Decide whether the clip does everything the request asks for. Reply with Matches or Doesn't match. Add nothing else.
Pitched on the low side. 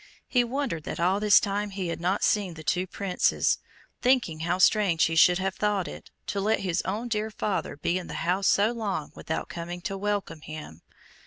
Doesn't match